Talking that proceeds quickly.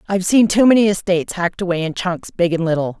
Yes: fast, 240 wpm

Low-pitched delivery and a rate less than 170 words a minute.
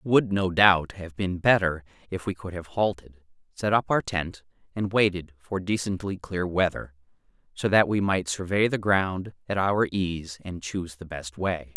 No: very low, 90 Hz; average, 190 wpm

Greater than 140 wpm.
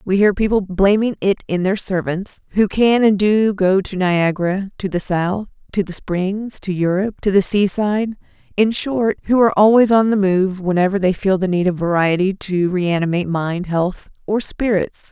Yes: average, 185 wpm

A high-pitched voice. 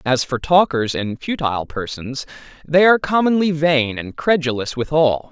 No: medium, 145 Hz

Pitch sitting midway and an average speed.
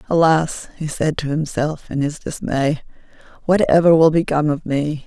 Yes: medium, 155 Hz; average, 165 wpm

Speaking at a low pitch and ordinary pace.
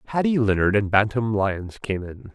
Yes: low, 105 Hz; average, 180 wpm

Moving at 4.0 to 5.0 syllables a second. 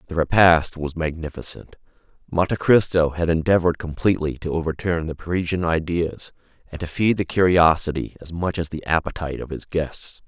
No: 5.5 syllables/s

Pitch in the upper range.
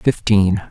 No: low, 100 Hz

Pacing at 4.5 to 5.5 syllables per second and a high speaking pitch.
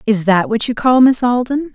Yes: 5.0 syllables/s; high, 235 Hz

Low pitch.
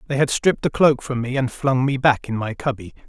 Yes: low, 130 Hz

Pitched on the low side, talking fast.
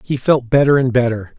Yes: low, 125 Hz; fast, 215 wpm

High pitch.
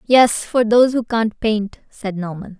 Yes: high, 220 Hz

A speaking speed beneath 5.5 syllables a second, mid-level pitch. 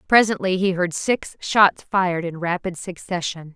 Yes: 4.5 syllables/s; medium, 180 Hz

